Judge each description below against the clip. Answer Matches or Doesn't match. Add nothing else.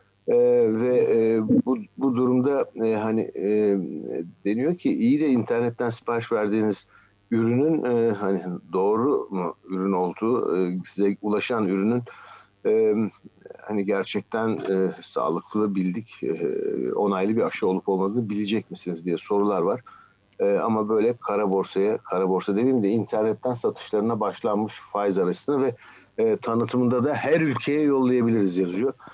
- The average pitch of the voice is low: Matches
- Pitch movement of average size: Matches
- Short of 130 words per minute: Doesn't match